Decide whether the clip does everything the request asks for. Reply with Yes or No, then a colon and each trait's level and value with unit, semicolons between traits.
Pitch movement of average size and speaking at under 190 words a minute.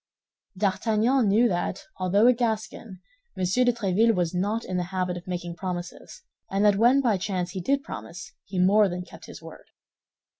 Yes: average, 3.9 semitones; average, 180 wpm